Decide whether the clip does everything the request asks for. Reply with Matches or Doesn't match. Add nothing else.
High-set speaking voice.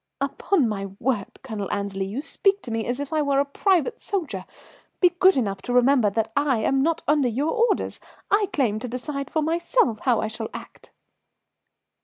Matches